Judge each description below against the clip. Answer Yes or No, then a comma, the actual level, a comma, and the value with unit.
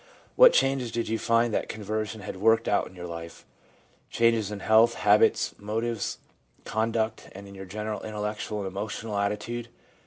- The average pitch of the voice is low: Yes, low, 110 Hz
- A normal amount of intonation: No, narrow, 2.1 semitones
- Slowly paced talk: No, average, 165 wpm